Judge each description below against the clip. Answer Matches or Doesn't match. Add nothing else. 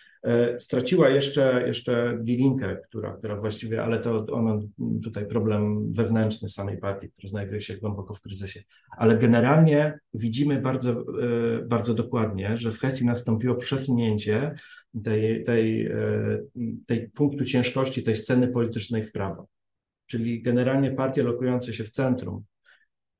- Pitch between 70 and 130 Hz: Matches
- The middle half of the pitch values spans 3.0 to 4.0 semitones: Doesn't match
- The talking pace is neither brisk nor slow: Matches